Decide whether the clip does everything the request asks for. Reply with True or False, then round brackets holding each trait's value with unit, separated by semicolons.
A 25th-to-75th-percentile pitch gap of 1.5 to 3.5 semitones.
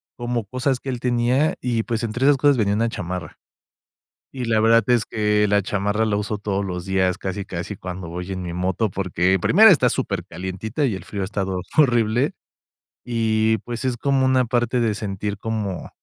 False (4.0 semitones)